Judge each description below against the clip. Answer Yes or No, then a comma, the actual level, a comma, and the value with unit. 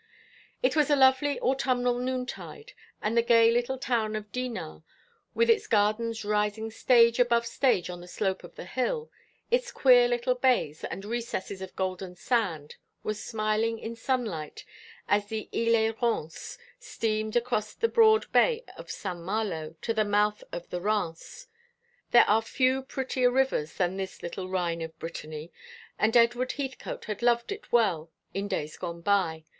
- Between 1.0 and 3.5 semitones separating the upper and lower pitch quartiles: No, average, 4.7 semitones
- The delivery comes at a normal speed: Yes, average, 160 wpm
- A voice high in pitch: Yes, high, 225 Hz